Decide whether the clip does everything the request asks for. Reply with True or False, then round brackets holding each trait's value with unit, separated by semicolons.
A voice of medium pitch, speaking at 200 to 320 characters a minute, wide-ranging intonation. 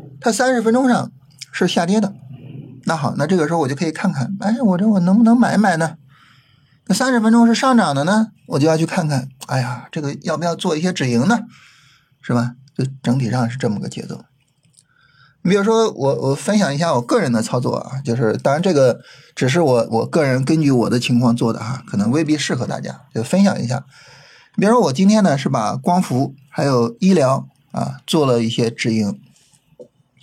True (145 Hz; 295 characters per minute; 6.8 semitones)